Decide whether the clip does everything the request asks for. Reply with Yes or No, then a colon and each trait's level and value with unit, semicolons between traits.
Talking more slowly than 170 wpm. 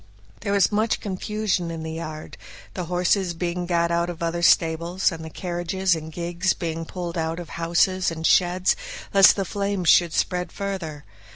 No: average, 175 wpm